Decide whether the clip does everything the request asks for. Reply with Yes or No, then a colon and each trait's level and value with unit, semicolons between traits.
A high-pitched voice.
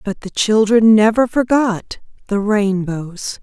Yes: high, 210 Hz